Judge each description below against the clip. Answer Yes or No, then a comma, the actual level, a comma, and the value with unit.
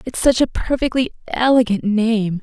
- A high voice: Yes, high, 235 Hz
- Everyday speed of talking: Yes, average, 150 wpm